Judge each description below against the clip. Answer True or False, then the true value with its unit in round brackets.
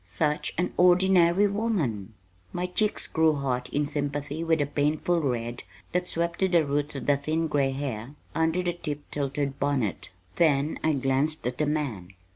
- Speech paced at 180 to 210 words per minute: False (170 wpm)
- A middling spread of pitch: True (3.6 semitones)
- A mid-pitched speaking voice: True (150 Hz)